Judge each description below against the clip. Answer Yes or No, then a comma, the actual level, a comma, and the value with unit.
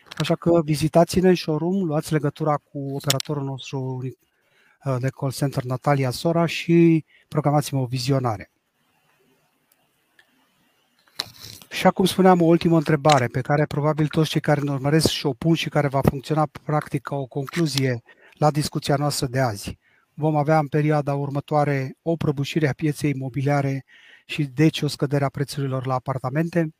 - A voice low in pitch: No, medium, 150 Hz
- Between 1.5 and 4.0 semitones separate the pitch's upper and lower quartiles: Yes, narrow, 2.4 semitones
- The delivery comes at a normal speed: Yes, average, 150 wpm